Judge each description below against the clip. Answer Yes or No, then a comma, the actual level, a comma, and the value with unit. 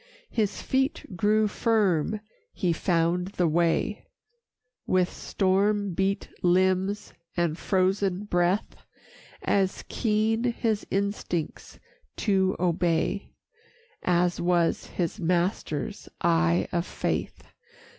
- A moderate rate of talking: No, slow, 95 wpm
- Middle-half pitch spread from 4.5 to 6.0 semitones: No, average, 2.9 semitones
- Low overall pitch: No, medium, 185 Hz